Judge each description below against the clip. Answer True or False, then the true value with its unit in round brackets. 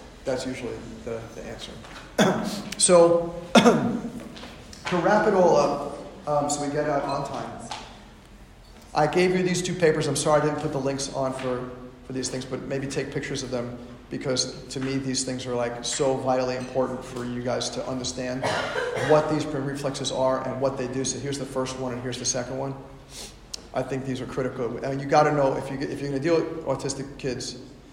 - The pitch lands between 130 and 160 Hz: True (135 Hz)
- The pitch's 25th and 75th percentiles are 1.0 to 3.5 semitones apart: True (2.6 semitones)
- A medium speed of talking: False (215 wpm)